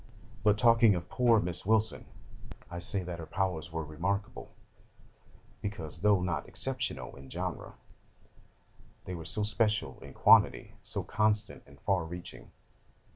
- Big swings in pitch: No, average, 4.1 semitones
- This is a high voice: No, very low, 95 Hz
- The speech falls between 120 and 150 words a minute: Yes, slow, 135 wpm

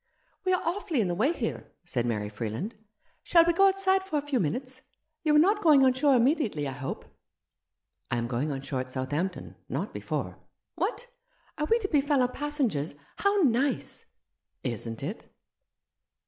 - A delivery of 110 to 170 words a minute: No, average, 195 wpm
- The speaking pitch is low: No, very high, 255 Hz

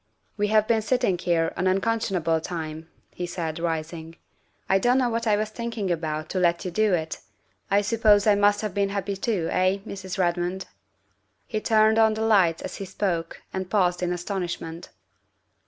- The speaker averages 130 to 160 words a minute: No, average, 195 wpm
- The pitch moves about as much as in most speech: Yes, average, 3.7 semitones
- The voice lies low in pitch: No, high, 190 Hz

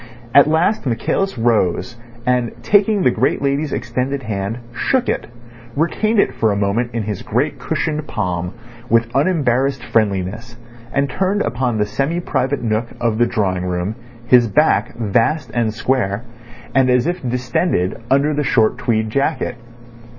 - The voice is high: No, low, 120 Hz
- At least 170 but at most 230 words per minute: No, average, 150 wpm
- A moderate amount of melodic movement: Yes, average, 4.4 semitones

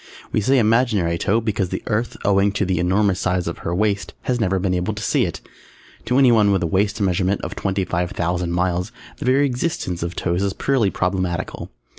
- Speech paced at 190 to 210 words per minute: Yes, fast, 205 wpm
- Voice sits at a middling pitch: No, very low, 95 Hz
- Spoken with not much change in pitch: No, average, 3.3 semitones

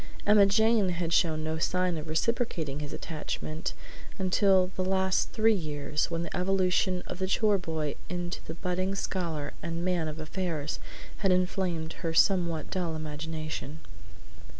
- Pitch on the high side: No, medium, 175 Hz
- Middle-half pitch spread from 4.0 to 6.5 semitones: No, average, 3.0 semitones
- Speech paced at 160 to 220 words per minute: No, average, 150 wpm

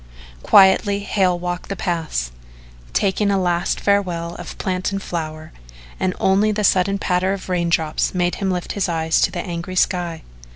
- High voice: No, medium, 180 Hz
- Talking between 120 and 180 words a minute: Yes, average, 165 wpm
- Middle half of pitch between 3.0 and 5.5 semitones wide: No, narrow, 2.4 semitones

